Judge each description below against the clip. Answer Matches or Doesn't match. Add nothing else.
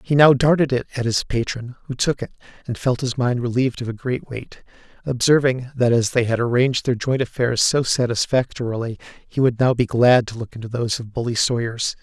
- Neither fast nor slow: Doesn't match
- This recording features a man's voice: Matches